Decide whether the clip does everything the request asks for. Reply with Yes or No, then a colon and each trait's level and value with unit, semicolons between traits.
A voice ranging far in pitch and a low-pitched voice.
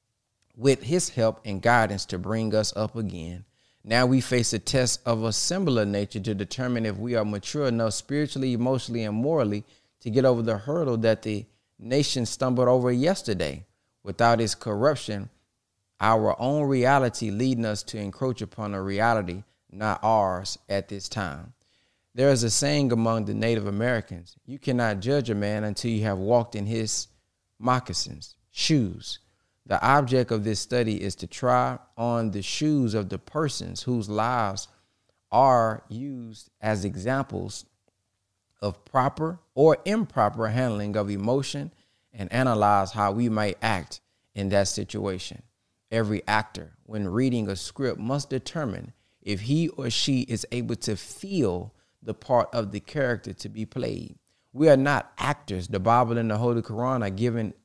No: average, 3.6 semitones; low, 110 Hz